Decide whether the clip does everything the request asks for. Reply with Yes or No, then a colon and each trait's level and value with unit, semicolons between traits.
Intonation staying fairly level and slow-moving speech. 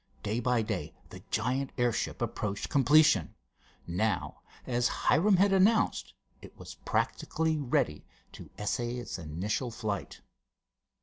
No: wide, 5.6 semitones; slow, 120 wpm